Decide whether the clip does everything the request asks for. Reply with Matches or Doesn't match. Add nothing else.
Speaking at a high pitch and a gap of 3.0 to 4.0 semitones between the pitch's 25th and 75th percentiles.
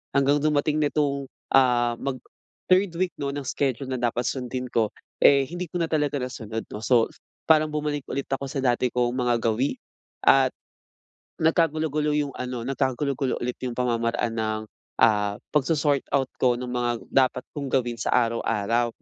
Doesn't match